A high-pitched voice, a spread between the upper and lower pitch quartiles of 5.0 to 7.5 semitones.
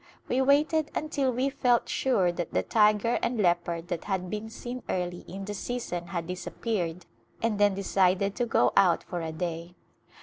Yes: high, 195 Hz; wide, 5.4 semitones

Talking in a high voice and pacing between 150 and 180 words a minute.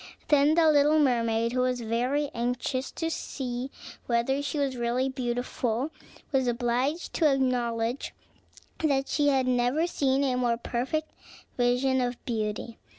No: very high, 255 Hz; average, 140 wpm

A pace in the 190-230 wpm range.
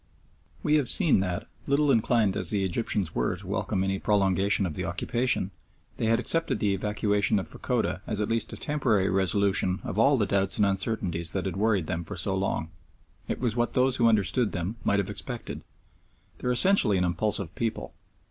Yes: average, 195 wpm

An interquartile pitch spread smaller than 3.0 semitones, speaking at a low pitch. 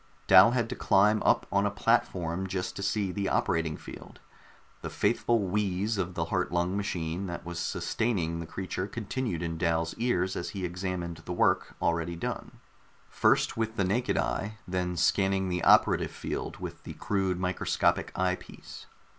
Yes: narrow, 2.5 semitones; very low, 90 Hz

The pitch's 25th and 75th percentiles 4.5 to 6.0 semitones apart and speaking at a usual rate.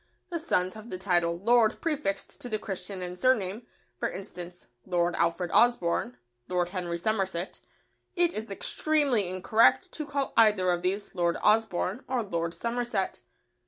Yes: average, 4.9 semitones; average, 150 wpm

